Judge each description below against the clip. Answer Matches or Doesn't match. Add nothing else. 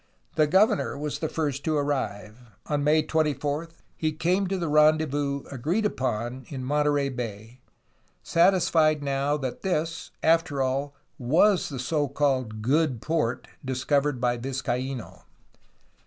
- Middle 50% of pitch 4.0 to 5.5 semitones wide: Doesn't match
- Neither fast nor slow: Doesn't match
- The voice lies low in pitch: Doesn't match